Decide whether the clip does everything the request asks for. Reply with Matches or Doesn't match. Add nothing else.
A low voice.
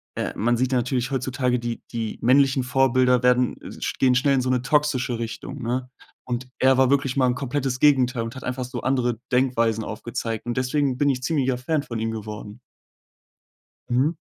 Matches